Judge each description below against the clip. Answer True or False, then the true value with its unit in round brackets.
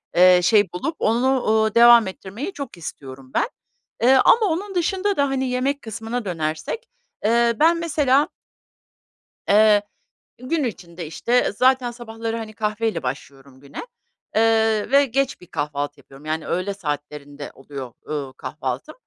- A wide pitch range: True (8.6 semitones)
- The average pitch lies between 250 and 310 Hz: False (220 Hz)